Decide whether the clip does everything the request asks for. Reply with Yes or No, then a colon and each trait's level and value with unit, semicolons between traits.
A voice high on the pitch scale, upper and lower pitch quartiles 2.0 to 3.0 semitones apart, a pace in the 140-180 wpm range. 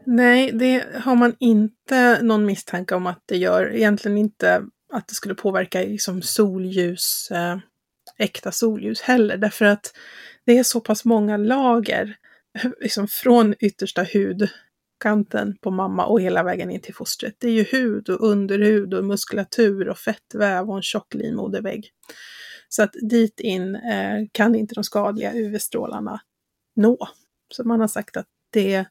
Yes: high, 215 Hz; average, 2.7 semitones; average, 150 wpm